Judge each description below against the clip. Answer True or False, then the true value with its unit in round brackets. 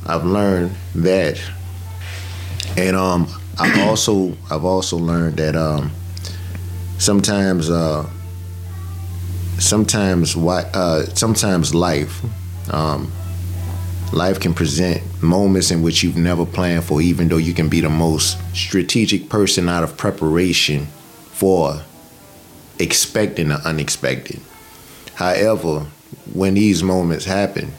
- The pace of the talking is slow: True (110 wpm)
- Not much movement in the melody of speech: True (1.8 semitones)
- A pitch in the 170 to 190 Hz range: False (90 Hz)